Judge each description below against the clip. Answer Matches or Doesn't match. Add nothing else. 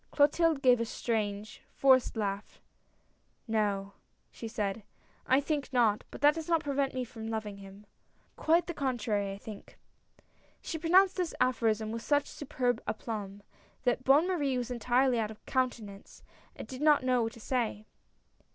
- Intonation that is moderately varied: Matches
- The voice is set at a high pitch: Matches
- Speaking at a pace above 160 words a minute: Matches